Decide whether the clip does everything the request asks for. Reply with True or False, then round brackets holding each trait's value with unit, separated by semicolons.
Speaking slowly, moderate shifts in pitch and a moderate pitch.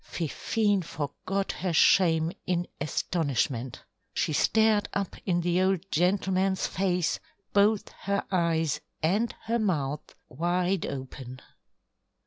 True (110 wpm; 3.5 semitones; 180 Hz)